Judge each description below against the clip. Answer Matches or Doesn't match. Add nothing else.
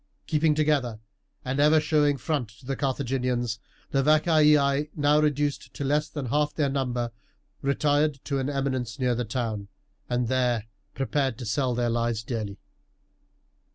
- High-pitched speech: Doesn't match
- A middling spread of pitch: Matches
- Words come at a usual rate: Matches